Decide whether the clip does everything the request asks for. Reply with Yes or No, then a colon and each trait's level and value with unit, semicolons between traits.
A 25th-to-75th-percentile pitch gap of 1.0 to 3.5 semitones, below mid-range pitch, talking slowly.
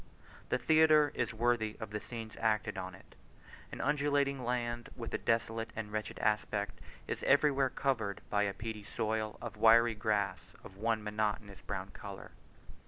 No: narrow, 2.5 semitones; low, 110 Hz; average, 160 wpm